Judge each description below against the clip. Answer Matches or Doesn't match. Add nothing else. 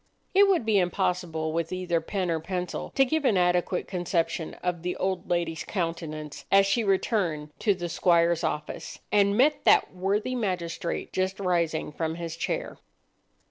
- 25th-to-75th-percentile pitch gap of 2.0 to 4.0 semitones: Matches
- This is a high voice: Doesn't match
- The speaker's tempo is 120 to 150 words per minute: Doesn't match